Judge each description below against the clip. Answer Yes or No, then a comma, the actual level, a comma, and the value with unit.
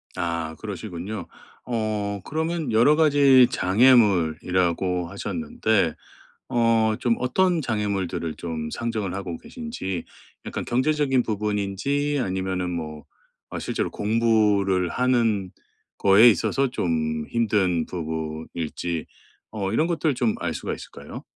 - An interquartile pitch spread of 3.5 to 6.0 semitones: Yes, wide, 5.6 semitones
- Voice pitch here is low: Yes, low, 105 Hz